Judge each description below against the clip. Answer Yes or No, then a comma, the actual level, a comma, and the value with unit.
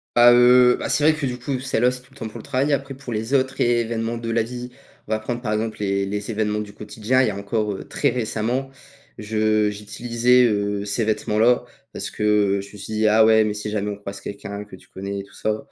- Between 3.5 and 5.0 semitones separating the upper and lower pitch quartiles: No, average, 2.9 semitones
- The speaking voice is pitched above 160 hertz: No, low, 110 Hz